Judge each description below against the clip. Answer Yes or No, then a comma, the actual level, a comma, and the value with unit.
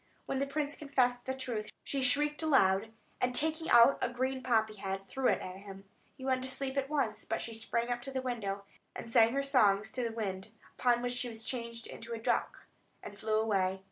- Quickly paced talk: Yes, fast, 215 wpm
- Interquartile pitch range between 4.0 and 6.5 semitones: No, average, 3.4 semitones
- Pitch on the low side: No, high, 240 Hz